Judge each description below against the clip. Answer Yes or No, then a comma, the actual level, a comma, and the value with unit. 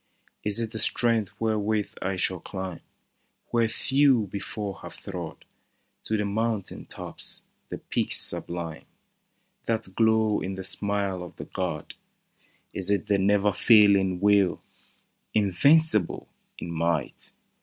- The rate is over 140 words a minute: No, slow, 135 wpm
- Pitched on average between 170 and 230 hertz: No, low, 100 Hz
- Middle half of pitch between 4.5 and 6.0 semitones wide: No, narrow, 2.6 semitones